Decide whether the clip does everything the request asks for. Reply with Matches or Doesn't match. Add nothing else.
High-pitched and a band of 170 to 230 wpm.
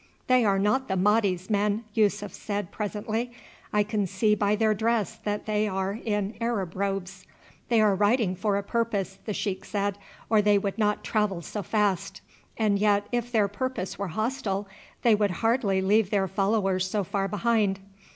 Matches